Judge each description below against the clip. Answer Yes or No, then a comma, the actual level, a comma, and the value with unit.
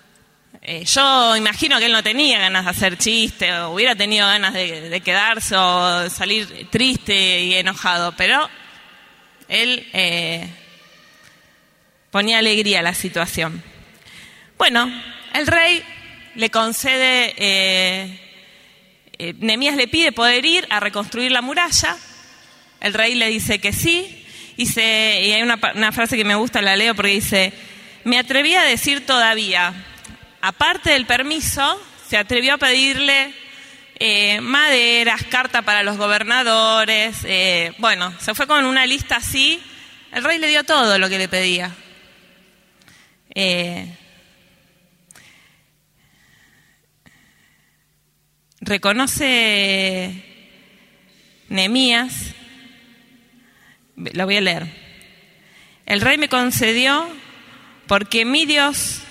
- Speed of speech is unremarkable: No, slow, 120 wpm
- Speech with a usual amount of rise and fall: Yes, average, 4.8 semitones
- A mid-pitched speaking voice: No, high, 215 Hz